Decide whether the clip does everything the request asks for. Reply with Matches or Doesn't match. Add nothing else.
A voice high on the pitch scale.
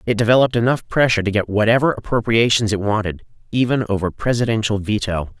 Doesn't match